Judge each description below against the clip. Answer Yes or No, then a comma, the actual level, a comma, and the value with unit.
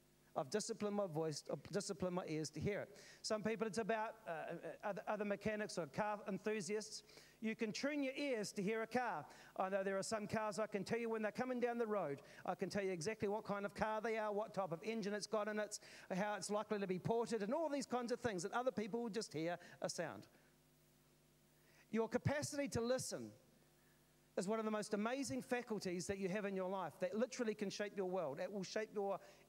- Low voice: No, high, 210 Hz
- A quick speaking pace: Yes, fast, 230 wpm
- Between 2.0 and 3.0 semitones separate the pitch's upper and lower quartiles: Yes, narrow, 2.5 semitones